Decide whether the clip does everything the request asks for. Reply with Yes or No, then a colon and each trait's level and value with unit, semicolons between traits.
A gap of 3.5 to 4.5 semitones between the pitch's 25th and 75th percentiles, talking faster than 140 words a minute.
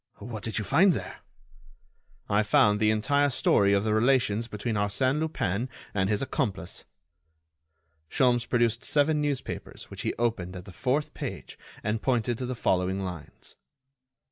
Yes: average, 4.2 semitones; average, 155 wpm